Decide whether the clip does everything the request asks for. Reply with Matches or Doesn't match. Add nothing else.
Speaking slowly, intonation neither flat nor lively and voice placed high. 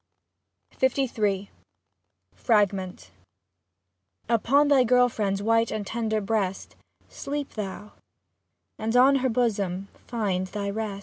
Matches